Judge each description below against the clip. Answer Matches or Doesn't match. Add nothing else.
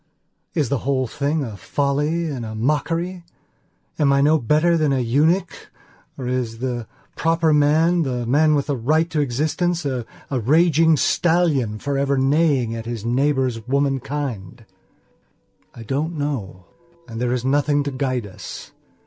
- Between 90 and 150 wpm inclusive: Matches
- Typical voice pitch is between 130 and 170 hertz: Matches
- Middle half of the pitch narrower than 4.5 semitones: Matches